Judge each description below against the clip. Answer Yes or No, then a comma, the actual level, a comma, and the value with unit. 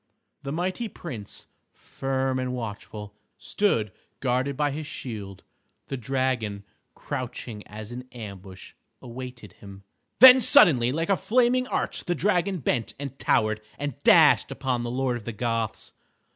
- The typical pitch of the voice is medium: No, low, 125 Hz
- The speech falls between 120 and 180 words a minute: Yes, average, 140 wpm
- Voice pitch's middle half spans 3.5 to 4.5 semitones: No, average, 4.9 semitones